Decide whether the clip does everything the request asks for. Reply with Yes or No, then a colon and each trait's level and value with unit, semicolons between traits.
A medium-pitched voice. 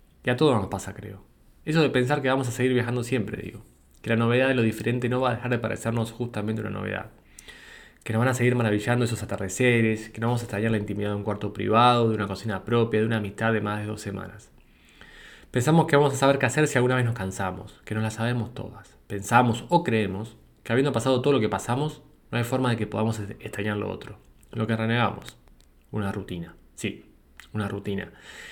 No: low, 110 Hz